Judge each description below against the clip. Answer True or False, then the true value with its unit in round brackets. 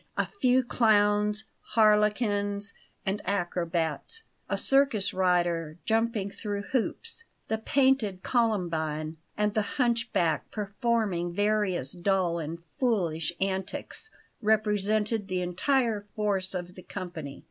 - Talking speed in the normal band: False (105 wpm)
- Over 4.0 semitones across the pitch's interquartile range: False (3.7 semitones)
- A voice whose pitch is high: True (205 Hz)